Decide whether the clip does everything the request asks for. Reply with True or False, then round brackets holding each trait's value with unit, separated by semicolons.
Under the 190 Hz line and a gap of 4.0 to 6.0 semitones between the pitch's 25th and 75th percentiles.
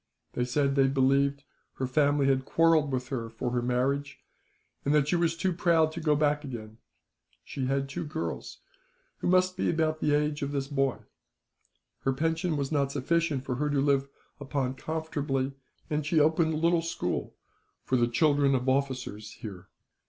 False (140 Hz; 3.0 semitones)